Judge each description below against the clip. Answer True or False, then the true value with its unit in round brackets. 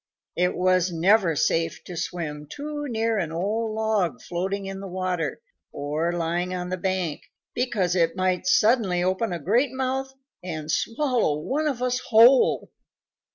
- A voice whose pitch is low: False (185 Hz)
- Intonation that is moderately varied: True (4.9 semitones)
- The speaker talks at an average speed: True (155 wpm)